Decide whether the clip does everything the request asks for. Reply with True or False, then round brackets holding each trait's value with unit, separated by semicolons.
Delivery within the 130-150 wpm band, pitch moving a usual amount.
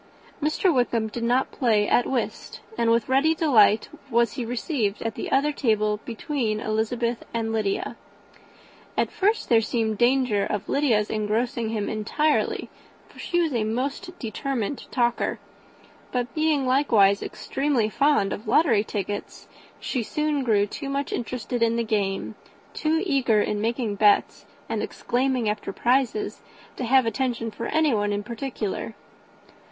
True (145 wpm; 4.0 semitones)